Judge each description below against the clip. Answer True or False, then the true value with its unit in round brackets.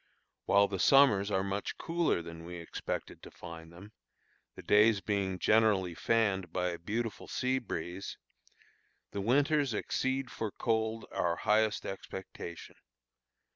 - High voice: False (100 Hz)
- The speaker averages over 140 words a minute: False (135 wpm)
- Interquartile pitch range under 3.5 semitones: False (4.1 semitones)